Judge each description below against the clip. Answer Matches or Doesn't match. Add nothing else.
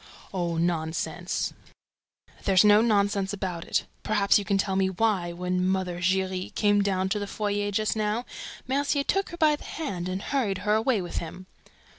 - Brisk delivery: Doesn't match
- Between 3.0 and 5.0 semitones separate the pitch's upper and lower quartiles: Doesn't match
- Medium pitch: Doesn't match